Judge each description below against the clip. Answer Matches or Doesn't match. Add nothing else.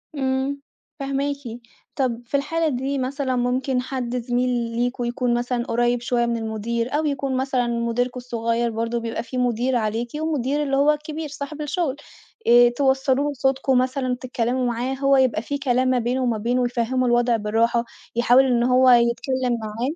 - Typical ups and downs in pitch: Doesn't match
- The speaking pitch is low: Doesn't match